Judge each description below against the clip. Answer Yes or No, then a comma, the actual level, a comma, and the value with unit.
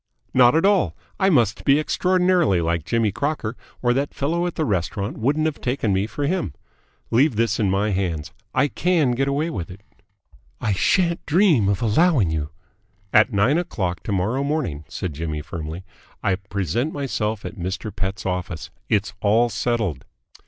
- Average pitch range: No, wide, 7.4 semitones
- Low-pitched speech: Yes, low, 110 Hz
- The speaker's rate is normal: Yes, average, 175 wpm